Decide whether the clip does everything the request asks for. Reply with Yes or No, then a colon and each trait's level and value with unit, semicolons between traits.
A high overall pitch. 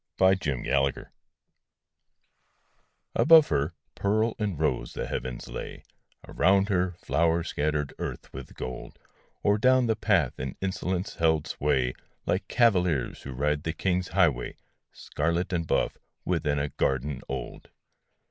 No: very low, 85 Hz